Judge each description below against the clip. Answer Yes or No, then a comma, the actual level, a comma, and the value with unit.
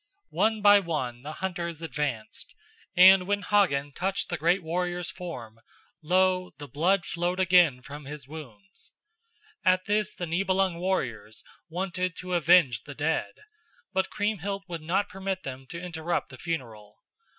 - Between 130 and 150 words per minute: Yes, average, 145 wpm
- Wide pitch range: No, average, 4.3 semitones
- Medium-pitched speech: Yes, medium, 175 Hz